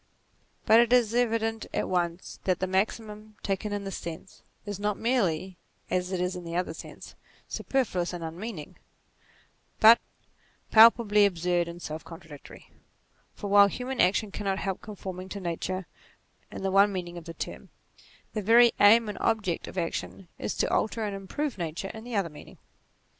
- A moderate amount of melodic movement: Yes, average, 3.6 semitones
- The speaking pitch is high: Yes, high, 195 Hz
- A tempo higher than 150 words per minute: Yes, average, 170 wpm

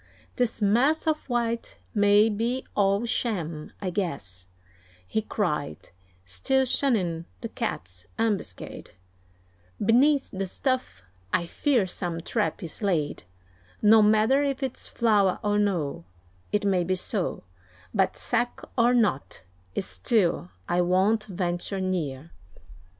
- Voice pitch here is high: Yes, high, 205 Hz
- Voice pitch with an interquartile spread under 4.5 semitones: No, average, 5.1 semitones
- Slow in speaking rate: Yes, slow, 120 wpm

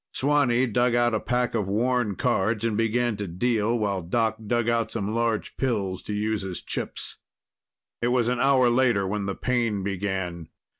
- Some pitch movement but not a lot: Yes, average, 3.1 semitones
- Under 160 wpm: No, average, 180 wpm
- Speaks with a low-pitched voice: Yes, low, 115 Hz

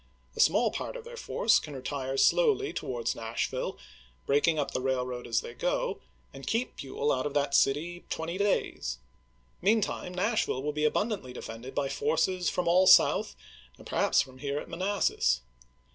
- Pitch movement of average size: No, wide, 7.4 semitones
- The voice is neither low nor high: Yes, medium, 150 Hz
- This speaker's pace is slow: No, average, 175 wpm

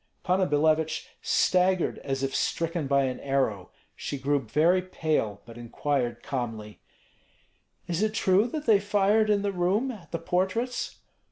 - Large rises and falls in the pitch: Yes, wide, 6.1 semitones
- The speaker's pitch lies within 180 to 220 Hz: No, medium, 165 Hz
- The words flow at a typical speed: Yes, average, 150 wpm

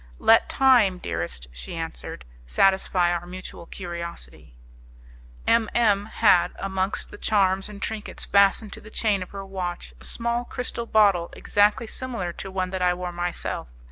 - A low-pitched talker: No, high, 190 Hz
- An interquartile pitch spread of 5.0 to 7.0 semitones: No, average, 3.3 semitones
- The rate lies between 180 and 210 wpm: No, average, 155 wpm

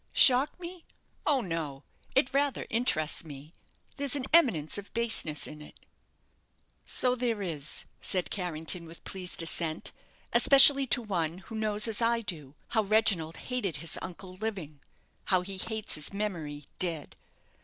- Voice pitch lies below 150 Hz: No, high, 195 Hz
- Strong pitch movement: Yes, wide, 6.3 semitones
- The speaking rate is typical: Yes, average, 145 wpm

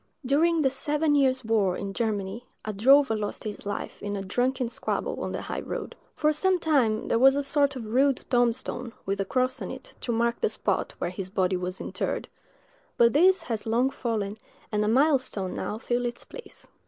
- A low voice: No, high, 240 Hz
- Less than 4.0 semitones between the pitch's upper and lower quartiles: No, average, 4.8 semitones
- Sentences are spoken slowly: No, average, 200 wpm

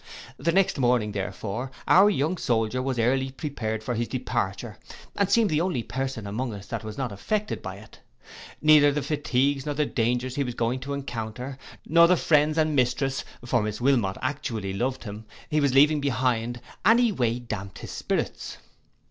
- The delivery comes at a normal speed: Yes, average, 175 wpm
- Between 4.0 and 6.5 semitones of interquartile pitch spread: Yes, average, 4.3 semitones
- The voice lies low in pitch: Yes, low, 130 Hz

